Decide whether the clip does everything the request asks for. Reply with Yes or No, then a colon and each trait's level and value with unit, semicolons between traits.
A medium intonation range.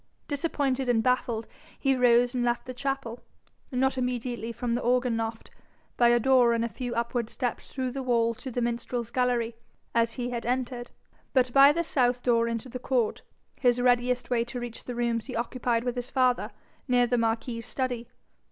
No: narrow, 1.3 semitones